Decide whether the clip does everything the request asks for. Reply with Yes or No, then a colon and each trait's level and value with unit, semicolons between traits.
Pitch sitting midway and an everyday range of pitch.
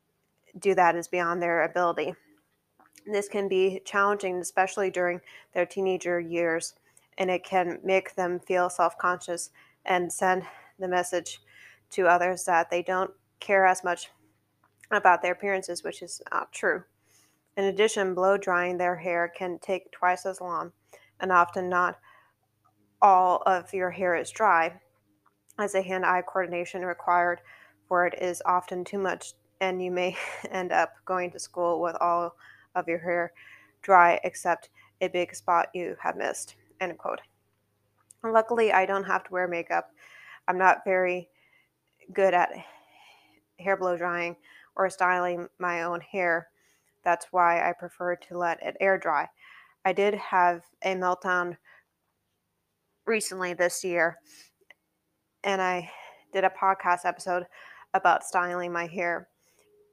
No: medium, 180 Hz; narrow, 1.5 semitones